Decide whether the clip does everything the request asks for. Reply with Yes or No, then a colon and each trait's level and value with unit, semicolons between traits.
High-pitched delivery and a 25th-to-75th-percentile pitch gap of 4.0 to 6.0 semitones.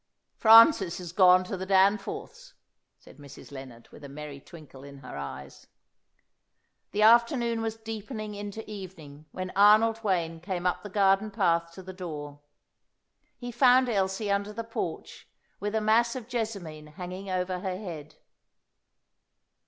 Yes: high, 195 Hz; average, 4.7 semitones